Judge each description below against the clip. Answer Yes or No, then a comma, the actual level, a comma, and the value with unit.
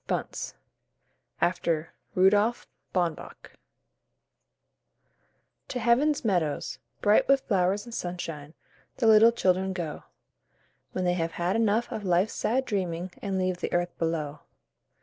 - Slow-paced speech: Yes, slow, 120 wpm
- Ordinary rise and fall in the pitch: Yes, average, 4.1 semitones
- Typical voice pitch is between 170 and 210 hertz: Yes, medium, 185 Hz